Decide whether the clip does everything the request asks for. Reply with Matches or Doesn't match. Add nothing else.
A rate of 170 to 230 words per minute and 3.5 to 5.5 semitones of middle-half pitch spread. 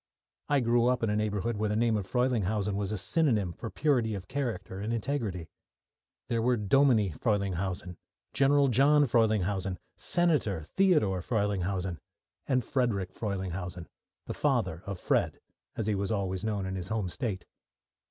Doesn't match